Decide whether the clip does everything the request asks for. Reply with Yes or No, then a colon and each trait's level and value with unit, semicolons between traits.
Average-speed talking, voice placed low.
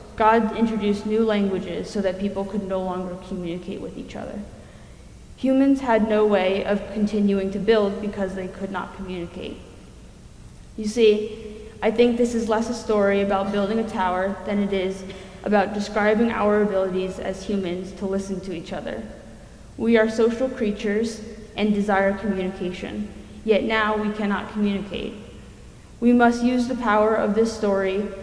No: average, 155 wpm; high, 205 Hz